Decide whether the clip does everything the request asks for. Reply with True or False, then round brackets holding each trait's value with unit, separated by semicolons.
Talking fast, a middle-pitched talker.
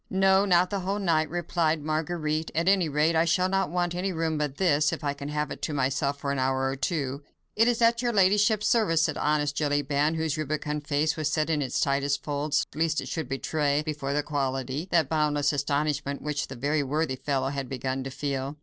True (215 wpm; 150 Hz)